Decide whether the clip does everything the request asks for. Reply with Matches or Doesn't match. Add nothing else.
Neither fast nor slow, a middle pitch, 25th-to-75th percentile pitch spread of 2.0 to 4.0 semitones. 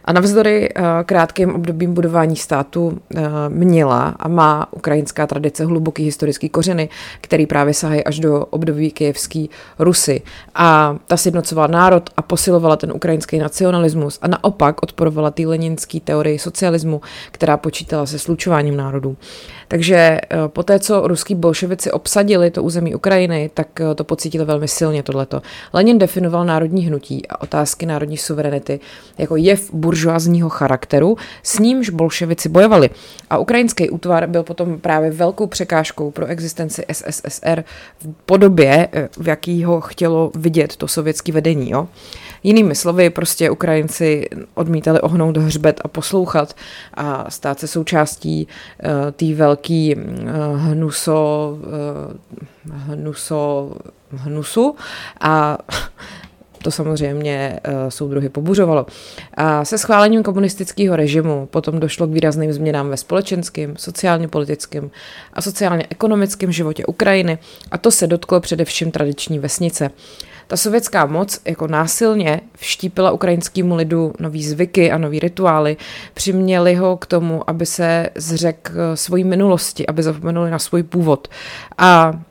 Matches